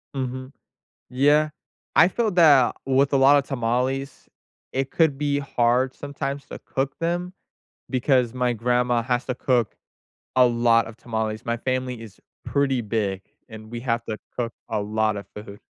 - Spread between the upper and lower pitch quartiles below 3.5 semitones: Yes, average, 2.9 semitones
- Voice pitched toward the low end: Yes, low, 125 Hz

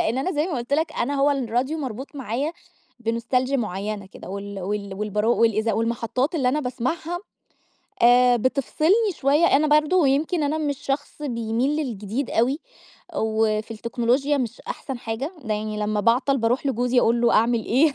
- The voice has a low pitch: No, very high, 250 Hz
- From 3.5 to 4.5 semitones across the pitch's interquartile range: Yes, average, 4.2 semitones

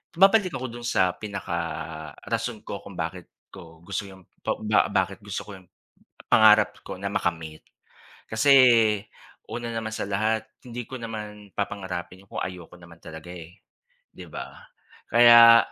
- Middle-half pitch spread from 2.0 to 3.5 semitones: No, average, 4.3 semitones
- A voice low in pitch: Yes, low, 105 Hz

